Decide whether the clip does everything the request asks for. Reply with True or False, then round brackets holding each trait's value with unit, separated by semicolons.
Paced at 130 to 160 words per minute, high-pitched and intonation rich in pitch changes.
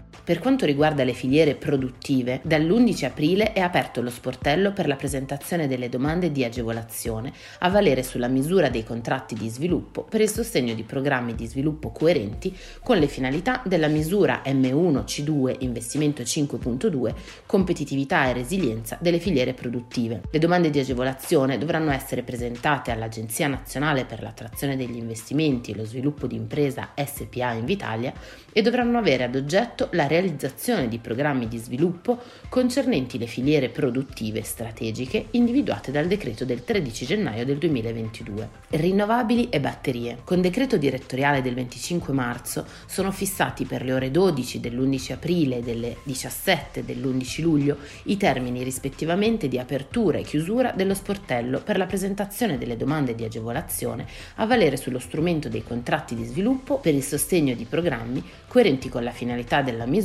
False (150 wpm; 135 Hz; 5.8 semitones)